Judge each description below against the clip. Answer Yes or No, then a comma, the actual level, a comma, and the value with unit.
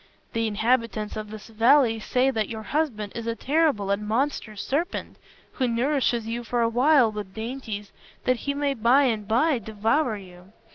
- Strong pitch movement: No, average, 3.8 semitones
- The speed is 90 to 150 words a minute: No, average, 175 wpm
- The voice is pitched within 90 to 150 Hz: No, high, 230 Hz